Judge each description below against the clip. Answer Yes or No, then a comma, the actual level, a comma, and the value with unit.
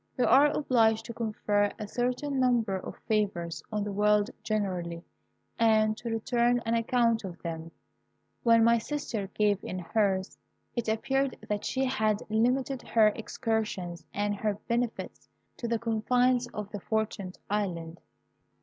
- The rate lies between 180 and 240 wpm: No, average, 145 wpm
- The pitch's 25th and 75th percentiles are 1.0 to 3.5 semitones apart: Yes, average, 2.7 semitones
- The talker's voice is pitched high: Yes, high, 220 Hz